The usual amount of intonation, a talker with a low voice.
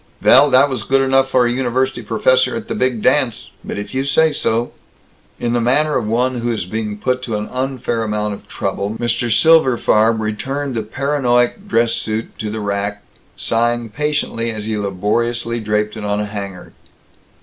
Yes: average, 3.6 semitones; low, 120 Hz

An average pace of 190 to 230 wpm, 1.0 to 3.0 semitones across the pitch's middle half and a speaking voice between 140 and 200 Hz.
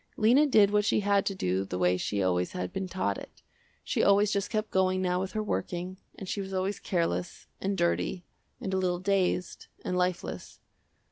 Yes: average, 200 wpm; narrow, 2.4 semitones; medium, 185 Hz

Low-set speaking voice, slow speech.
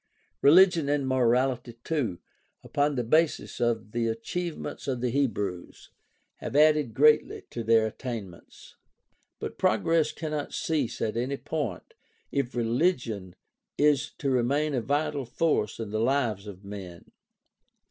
Yes: low, 125 Hz; slow, 130 wpm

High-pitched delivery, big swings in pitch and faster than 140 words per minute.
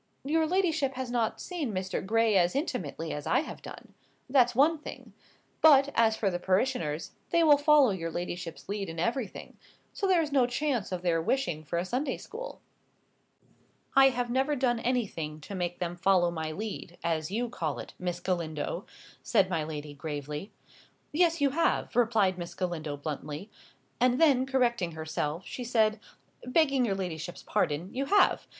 Yes: high, 215 Hz; wide, 7.7 semitones; average, 170 wpm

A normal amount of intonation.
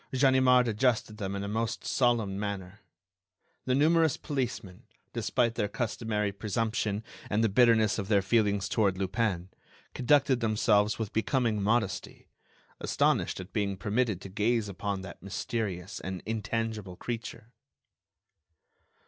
Yes: average, 3.0 semitones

